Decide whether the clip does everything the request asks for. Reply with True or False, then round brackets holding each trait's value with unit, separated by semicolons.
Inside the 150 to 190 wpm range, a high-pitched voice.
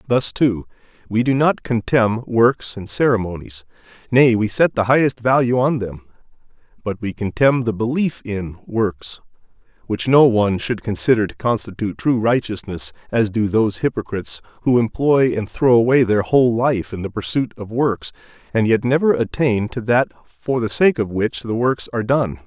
False (170 wpm; 115 Hz)